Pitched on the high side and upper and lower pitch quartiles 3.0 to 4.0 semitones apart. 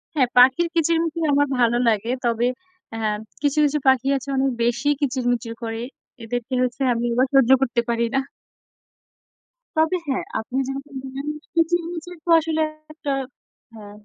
No: very high, 265 Hz; average, 4.4 semitones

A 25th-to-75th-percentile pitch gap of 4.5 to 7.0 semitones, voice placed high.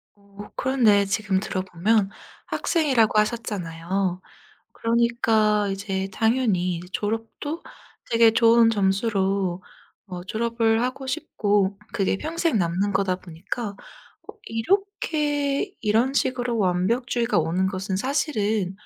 No: average, 3.7 semitones; high, 215 Hz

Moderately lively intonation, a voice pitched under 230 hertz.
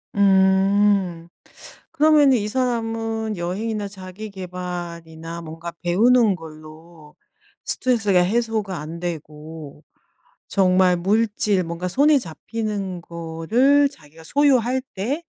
Yes: average, 4.9 semitones; high, 190 Hz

